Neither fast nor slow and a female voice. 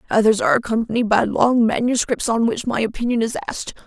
Yes: average, 185 wpm; female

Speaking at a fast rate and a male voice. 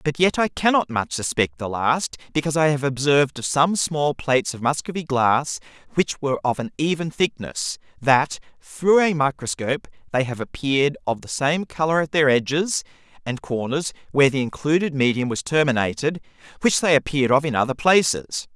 No: average, 175 wpm; male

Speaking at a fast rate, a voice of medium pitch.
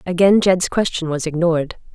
No: average, 155 wpm; medium, 170 Hz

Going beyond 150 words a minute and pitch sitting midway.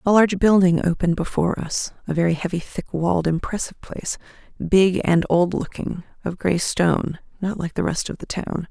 Yes: average, 185 wpm; medium, 180 Hz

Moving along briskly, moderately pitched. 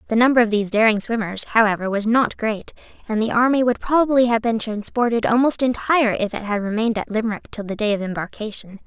No: fast, 210 wpm; high, 225 Hz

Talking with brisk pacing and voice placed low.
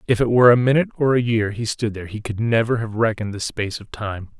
Yes: fast, 275 wpm; low, 115 Hz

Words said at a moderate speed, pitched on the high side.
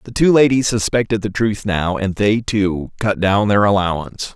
No: average, 195 wpm; low, 105 Hz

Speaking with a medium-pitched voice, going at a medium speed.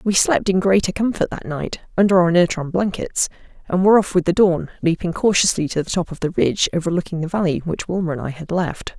No: medium, 180 Hz; fast, 225 wpm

